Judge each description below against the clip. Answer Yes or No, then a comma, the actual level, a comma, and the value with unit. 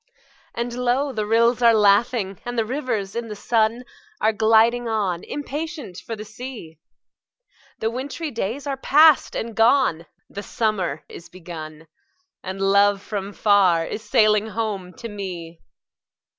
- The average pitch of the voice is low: No, high, 220 Hz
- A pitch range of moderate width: Yes, average, 3.7 semitones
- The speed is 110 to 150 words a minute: Yes, average, 145 wpm